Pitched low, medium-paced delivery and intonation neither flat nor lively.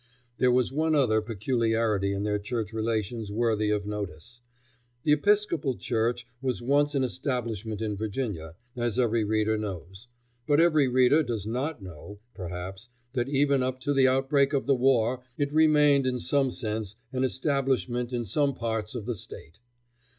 Yes: low, 120 Hz; average, 160 wpm; average, 4.0 semitones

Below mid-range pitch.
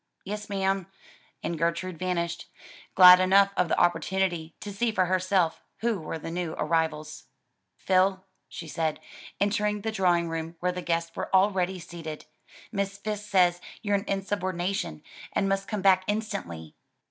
No: medium, 185 Hz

